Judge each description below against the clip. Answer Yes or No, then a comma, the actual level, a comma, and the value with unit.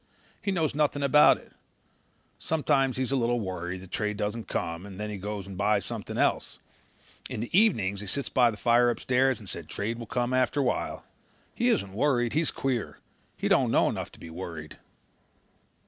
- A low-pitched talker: Yes, low, 120 Hz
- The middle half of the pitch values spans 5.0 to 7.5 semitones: Yes, average, 5.3 semitones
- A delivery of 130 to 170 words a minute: No, average, 195 wpm